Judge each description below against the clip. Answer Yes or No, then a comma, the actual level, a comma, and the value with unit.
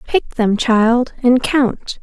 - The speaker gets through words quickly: No, average, 150 wpm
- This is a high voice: Yes, high, 245 Hz